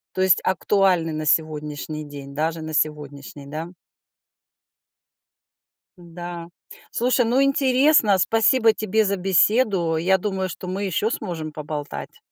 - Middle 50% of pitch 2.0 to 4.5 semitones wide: No, average, 5.2 semitones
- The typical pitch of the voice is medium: Yes, medium, 180 Hz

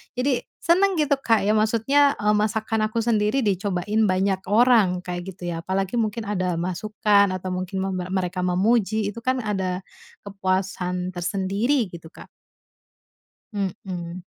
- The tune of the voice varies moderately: Yes, average, 3.1 semitones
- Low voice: No, high, 200 Hz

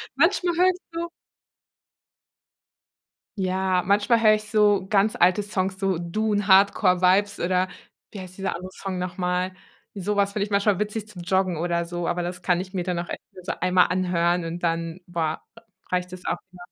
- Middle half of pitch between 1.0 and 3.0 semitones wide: Yes, narrow, 2.4 semitones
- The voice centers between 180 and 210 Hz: Yes, medium, 185 Hz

